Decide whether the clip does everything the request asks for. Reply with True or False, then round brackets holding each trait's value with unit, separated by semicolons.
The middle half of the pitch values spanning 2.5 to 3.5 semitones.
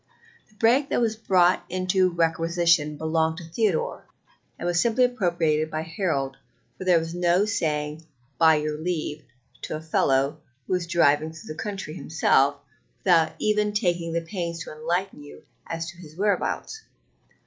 True (2.9 semitones)